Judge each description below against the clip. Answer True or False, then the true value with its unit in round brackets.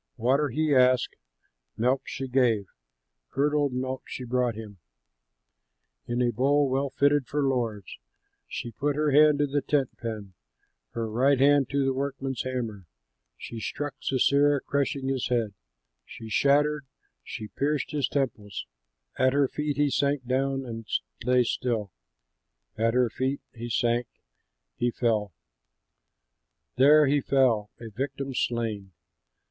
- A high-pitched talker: False (130 Hz)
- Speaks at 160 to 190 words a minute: False (135 wpm)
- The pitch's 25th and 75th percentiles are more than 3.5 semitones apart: False (3.2 semitones)